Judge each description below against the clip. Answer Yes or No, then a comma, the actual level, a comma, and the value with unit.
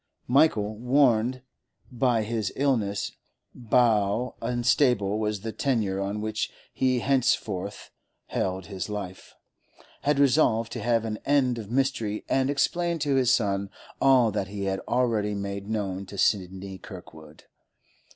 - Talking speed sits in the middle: No, slow, 130 wpm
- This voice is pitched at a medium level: No, low, 110 Hz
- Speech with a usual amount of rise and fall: Yes, average, 4.2 semitones